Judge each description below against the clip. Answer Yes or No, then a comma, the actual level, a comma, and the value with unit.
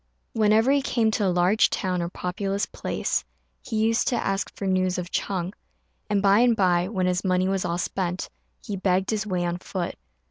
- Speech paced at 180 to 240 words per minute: Yes, average, 200 wpm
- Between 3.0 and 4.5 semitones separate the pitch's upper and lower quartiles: No, narrow, 2.6 semitones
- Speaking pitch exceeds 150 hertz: Yes, high, 190 Hz